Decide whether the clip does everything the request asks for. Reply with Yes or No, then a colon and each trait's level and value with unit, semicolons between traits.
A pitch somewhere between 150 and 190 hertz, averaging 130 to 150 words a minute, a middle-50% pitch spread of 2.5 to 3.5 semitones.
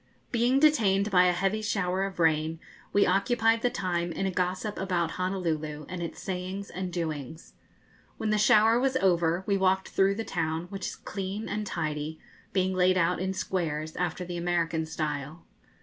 No: medium, 185 Hz; average, 175 wpm; average, 3.0 semitones